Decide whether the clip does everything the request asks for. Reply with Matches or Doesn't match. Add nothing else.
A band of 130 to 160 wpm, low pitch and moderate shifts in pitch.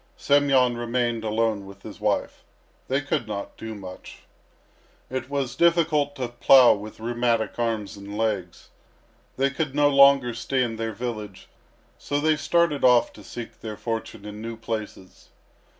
Matches